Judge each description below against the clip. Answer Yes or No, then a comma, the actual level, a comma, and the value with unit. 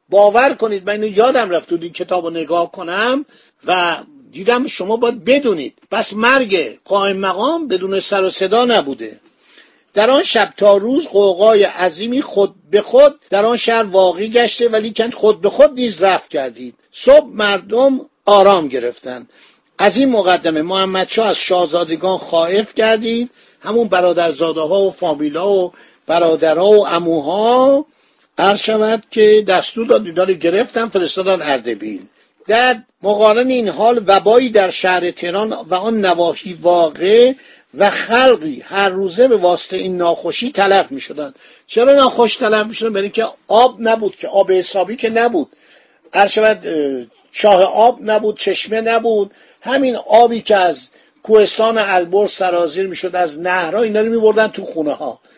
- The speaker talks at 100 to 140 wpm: No, average, 150 wpm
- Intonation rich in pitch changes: No, average, 4.0 semitones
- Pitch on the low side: No, high, 205 Hz